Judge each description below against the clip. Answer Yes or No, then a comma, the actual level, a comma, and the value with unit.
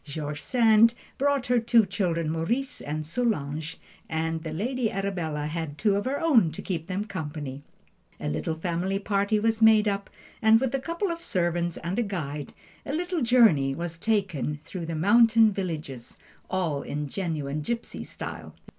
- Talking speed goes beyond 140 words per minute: Yes, average, 165 wpm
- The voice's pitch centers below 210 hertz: Yes, medium, 185 Hz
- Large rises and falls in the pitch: Yes, wide, 6.2 semitones